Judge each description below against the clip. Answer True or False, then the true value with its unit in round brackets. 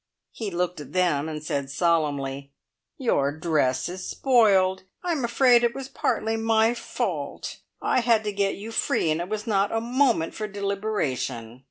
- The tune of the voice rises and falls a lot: True (6.4 semitones)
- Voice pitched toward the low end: False (195 Hz)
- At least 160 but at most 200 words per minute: True (165 wpm)